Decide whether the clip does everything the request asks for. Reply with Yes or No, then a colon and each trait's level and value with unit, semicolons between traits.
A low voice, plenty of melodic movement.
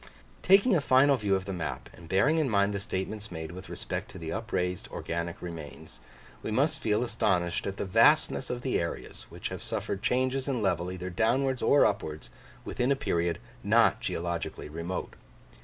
Yes: low, 100 Hz; wide, 6.8 semitones